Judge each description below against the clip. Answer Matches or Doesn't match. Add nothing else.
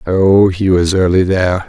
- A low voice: Matches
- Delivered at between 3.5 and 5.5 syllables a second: Matches